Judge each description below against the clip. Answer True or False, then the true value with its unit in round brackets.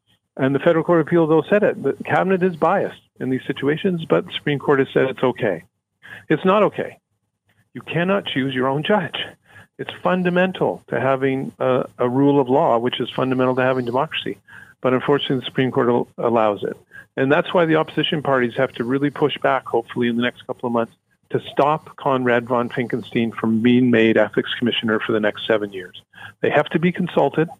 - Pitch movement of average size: True (4.1 semitones)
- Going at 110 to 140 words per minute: False (200 wpm)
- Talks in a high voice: False (130 Hz)